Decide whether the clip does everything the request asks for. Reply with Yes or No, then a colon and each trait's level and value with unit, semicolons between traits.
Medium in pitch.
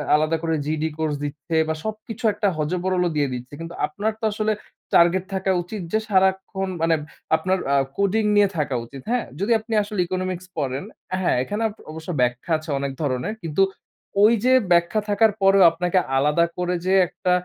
Yes: medium, 180 Hz